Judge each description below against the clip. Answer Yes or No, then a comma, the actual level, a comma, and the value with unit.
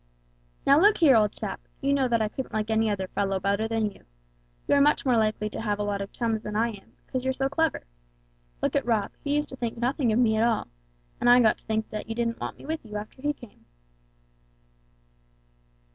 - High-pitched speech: Yes, high, 230 Hz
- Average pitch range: Yes, average, 3.7 semitones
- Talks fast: Yes, fast, 225 wpm